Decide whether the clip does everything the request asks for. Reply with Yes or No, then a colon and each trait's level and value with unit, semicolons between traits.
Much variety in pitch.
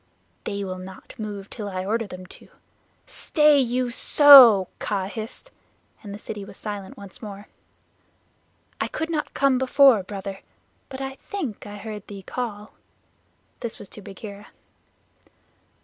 No: average, 4.3 semitones